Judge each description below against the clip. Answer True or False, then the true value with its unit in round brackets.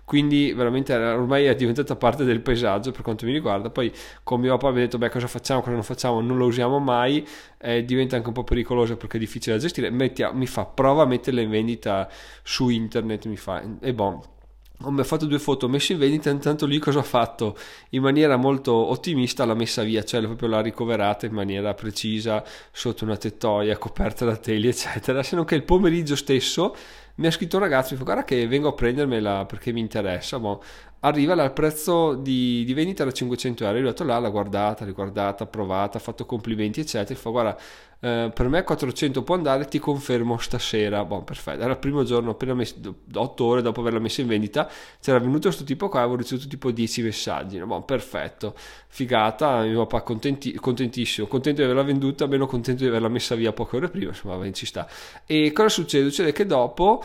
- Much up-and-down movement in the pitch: False (3.5 semitones)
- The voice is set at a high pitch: False (120 Hz)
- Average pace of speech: False (205 wpm)